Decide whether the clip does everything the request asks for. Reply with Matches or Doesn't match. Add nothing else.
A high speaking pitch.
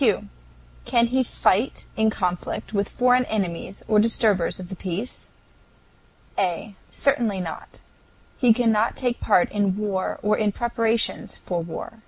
Matches